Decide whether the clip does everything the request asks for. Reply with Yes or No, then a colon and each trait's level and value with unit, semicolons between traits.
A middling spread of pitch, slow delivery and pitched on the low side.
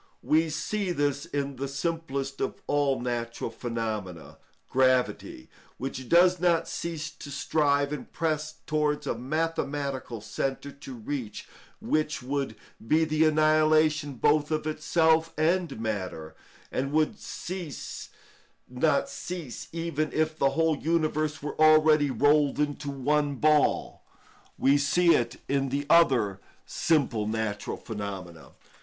No: average, 3.2 semitones; slow, 125 wpm; medium, 145 Hz